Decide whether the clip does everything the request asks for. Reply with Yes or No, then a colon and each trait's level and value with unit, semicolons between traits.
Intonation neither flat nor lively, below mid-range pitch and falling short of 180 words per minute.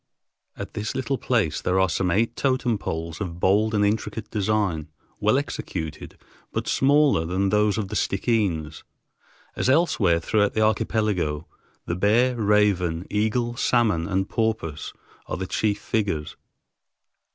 Yes: average, 4.2 semitones; low, 105 Hz; average, 140 wpm